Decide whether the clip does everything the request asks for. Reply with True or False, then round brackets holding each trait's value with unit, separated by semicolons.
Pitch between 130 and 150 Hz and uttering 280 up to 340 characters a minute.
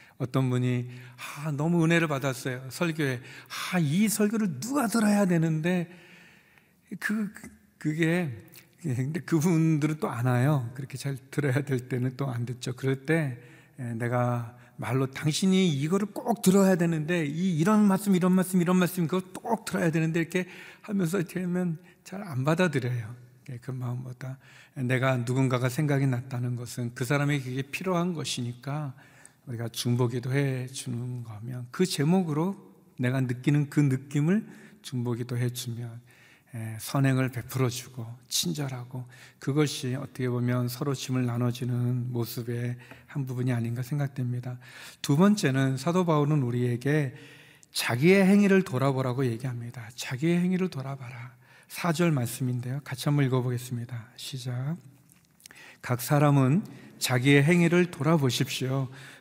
True (135 Hz; 300 characters per minute)